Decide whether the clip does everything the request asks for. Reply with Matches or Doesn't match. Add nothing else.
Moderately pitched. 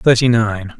Doesn't match